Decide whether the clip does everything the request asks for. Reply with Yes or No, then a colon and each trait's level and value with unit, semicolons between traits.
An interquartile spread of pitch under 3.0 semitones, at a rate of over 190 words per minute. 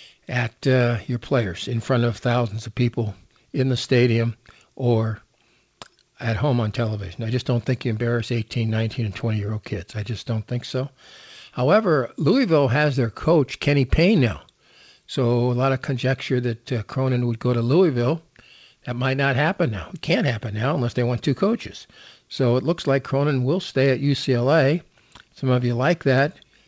No: narrow, 2.6 semitones; average, 185 wpm